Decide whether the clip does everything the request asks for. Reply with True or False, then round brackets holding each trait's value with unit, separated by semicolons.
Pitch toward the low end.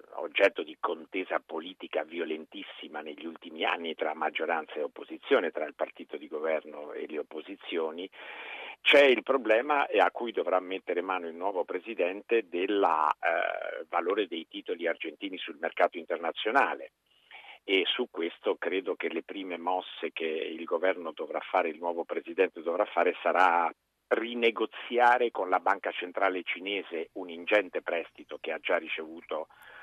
False (385 Hz)